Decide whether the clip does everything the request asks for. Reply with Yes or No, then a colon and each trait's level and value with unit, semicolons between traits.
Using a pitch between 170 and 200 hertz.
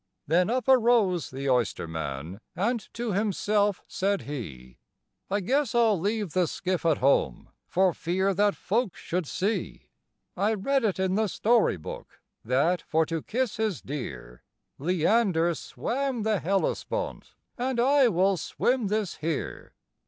Yes: high, 190 Hz